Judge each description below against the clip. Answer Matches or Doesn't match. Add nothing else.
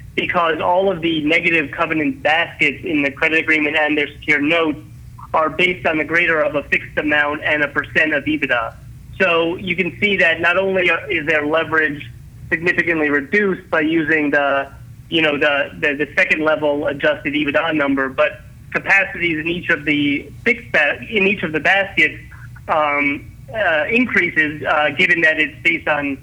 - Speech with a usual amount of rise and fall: Matches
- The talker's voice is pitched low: Doesn't match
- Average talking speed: Matches